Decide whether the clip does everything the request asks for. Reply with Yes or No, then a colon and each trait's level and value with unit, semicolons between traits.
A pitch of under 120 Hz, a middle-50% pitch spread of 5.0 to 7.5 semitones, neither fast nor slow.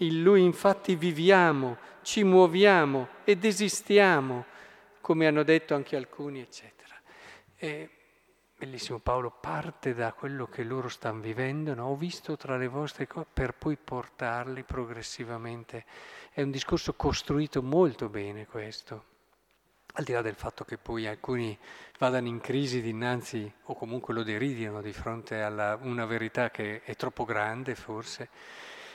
No: low, 130 Hz; average, 5.3 semitones; average, 140 wpm